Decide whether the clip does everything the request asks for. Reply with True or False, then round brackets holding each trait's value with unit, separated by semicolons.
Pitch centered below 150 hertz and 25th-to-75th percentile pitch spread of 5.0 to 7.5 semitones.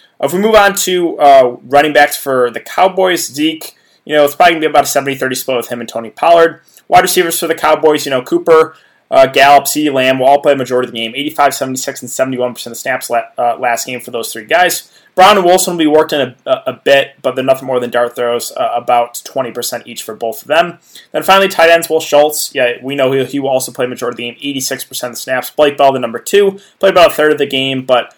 False (140 Hz; 4.6 semitones)